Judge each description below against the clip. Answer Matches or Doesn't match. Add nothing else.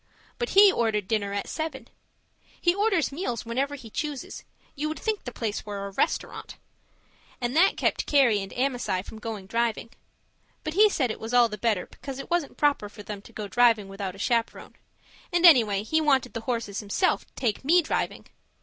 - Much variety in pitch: Matches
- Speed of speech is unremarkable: Matches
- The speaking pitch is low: Doesn't match